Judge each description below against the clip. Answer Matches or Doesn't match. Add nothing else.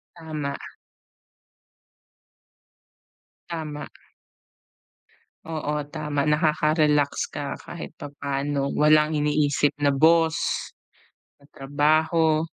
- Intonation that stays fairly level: Matches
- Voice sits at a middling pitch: Matches